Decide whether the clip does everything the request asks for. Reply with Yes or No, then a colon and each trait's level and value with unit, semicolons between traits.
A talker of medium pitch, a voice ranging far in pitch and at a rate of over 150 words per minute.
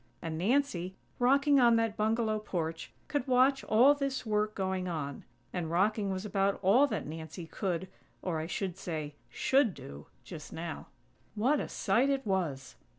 No: high, 195 Hz; wide, 6.5 semitones; average, 160 wpm